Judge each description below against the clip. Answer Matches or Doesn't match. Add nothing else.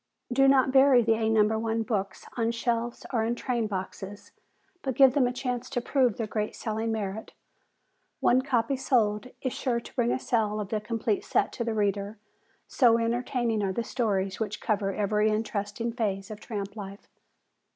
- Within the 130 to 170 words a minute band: Doesn't match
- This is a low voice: Doesn't match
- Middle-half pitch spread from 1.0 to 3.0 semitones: Matches